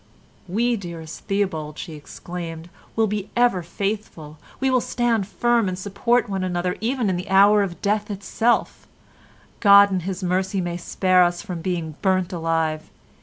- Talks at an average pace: Yes, average, 160 wpm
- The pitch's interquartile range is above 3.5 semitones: No, average, 3.2 semitones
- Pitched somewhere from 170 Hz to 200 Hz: Yes, high, 190 Hz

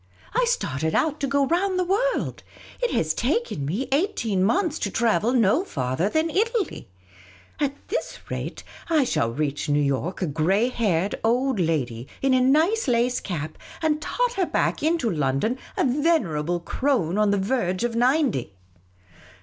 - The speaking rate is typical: Yes, average, 160 wpm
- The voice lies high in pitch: Yes, high, 240 Hz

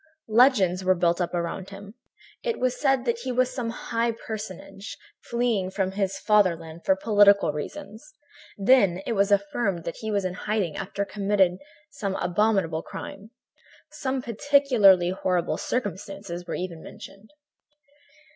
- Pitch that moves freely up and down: No, average, 3.8 semitones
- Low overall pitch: No, high, 200 Hz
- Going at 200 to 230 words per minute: No, average, 145 wpm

